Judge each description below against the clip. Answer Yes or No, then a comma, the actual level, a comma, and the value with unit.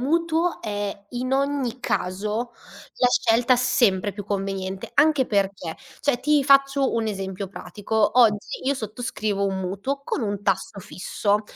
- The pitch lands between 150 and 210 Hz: No, high, 220 Hz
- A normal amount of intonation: Yes, average, 4.8 semitones